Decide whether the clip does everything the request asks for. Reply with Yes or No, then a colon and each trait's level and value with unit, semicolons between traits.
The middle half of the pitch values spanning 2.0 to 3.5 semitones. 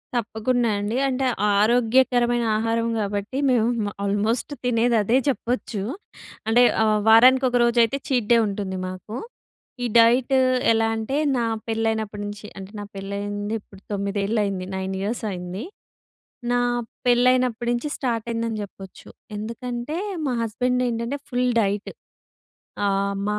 Yes: average, 3.1 semitones